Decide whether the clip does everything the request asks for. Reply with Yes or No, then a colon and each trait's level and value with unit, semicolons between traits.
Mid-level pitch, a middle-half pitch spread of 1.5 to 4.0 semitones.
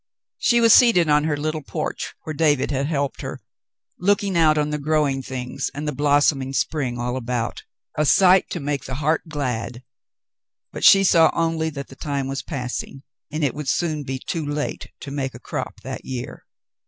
Yes: medium, 145 Hz; average, 2.9 semitones